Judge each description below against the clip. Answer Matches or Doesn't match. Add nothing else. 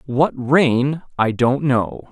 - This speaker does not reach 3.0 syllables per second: Matches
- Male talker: Matches